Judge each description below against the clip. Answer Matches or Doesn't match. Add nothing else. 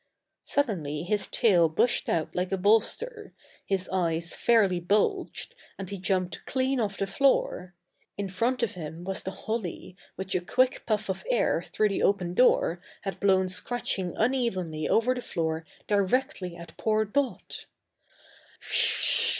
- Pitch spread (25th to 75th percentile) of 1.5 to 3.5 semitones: Doesn't match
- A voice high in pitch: Matches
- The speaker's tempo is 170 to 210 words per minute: Doesn't match